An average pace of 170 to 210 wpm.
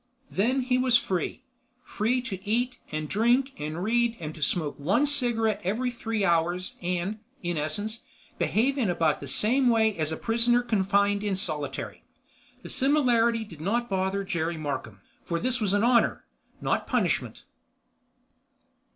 No: average, 145 wpm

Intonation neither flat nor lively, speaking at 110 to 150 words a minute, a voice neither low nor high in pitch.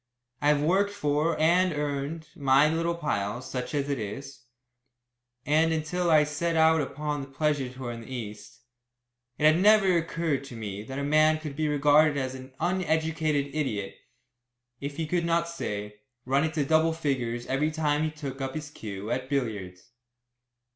No: average, 3.3 semitones; average, 170 wpm; medium, 150 Hz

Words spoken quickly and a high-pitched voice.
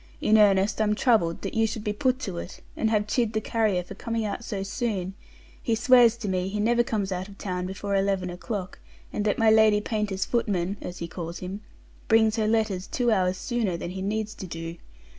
Yes: fast, 215 wpm; high, 210 Hz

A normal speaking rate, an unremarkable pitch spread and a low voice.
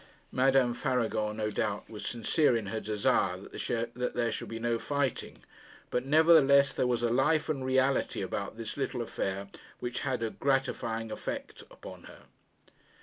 Yes: average, 155 wpm; average, 3.3 semitones; low, 120 Hz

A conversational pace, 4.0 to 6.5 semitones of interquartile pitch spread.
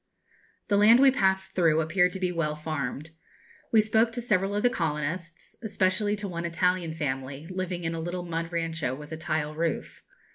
No: average, 185 wpm; average, 3.3 semitones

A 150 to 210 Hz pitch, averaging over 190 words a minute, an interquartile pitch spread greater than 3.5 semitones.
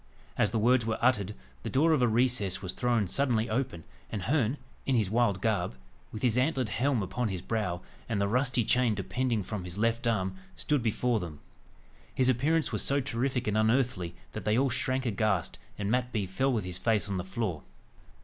No: low, 115 Hz; average, 200 wpm; average, 4.1 semitones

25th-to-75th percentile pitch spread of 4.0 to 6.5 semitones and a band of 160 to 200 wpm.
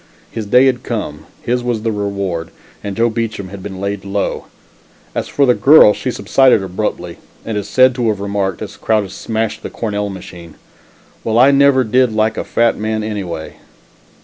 No: average, 3.2 semitones; average, 180 wpm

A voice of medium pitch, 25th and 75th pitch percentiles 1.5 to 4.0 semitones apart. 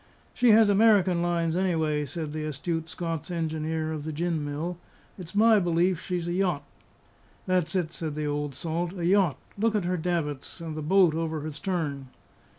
Yes: medium, 165 Hz; average, 2.7 semitones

